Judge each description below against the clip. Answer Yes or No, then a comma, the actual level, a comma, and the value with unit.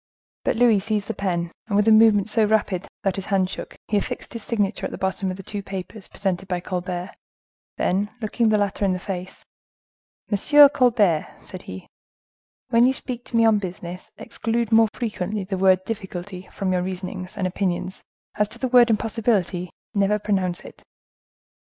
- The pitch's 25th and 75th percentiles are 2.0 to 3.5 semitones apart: Yes, average, 3.1 semitones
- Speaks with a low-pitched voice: No, high, 200 Hz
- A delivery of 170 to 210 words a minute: Yes, average, 175 wpm